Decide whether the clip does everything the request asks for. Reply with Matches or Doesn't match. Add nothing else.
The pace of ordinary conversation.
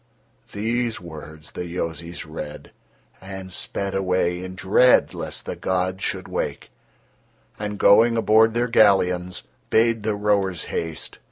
Doesn't match